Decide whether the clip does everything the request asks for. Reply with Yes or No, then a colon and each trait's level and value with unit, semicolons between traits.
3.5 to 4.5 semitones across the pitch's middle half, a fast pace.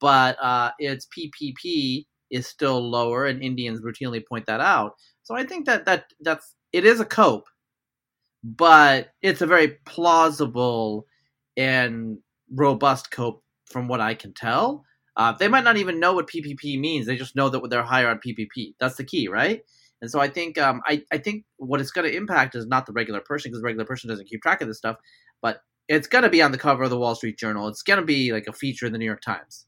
Yes: average, 4.2 semitones; fast, 220 wpm